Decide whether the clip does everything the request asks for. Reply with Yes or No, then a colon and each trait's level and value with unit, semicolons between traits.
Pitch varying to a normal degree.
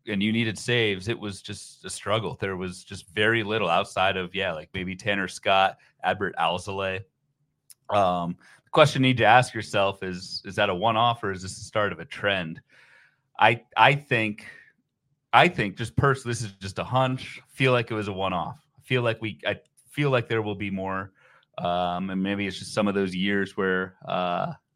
Yes: average, 3.5 semitones